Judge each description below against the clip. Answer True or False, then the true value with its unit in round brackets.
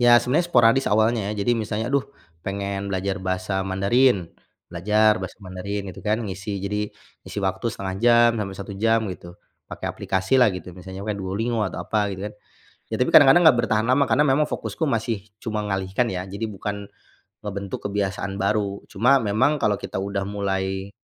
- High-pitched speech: False (105 Hz)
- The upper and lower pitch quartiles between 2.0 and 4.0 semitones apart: True (2.9 semitones)